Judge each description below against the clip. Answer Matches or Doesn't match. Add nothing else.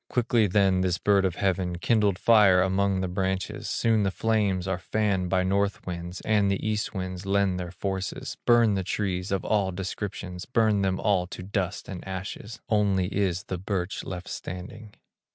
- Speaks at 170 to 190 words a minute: Matches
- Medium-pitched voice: Doesn't match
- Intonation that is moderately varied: Doesn't match